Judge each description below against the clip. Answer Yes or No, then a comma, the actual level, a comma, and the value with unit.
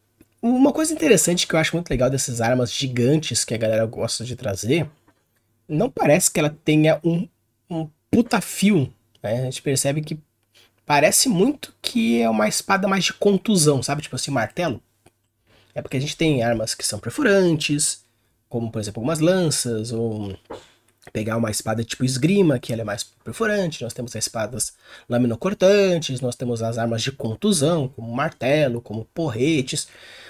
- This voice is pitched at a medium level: No, low, 130 Hz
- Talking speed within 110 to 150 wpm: No, average, 165 wpm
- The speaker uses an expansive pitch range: Yes, wide, 6.1 semitones